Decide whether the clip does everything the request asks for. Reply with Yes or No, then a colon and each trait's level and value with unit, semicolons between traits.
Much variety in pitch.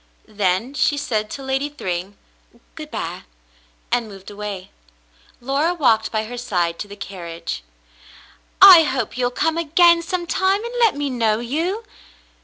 Yes: wide, 7.7 semitones